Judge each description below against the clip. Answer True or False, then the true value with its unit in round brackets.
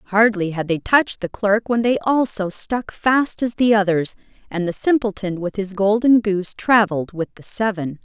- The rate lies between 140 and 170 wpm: False (185 wpm)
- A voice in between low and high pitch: False (205 Hz)